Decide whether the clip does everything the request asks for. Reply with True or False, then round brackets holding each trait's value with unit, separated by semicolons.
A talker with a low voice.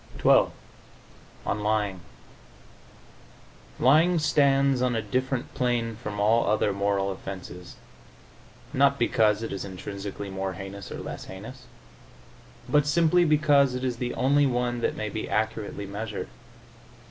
True (115 Hz)